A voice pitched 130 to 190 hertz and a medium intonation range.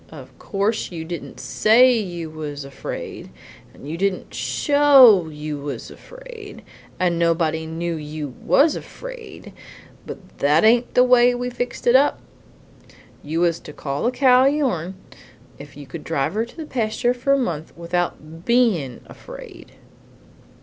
No: medium, 185 Hz; wide, 7.8 semitones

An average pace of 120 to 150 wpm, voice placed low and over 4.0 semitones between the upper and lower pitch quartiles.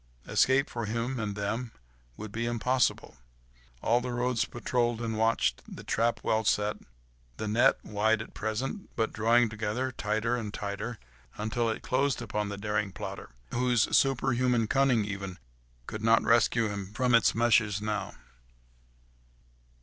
No: average, 145 wpm; low, 115 Hz; narrow, 2.4 semitones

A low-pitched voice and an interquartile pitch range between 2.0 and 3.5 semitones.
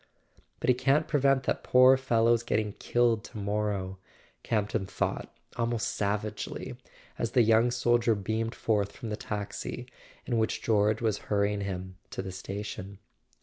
Yes: low, 110 Hz; average, 2.8 semitones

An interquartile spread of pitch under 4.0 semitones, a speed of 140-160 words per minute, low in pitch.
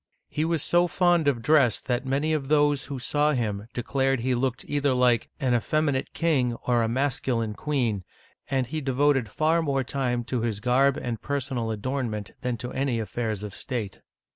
No: average, 3.3 semitones; average, 185 wpm; low, 130 Hz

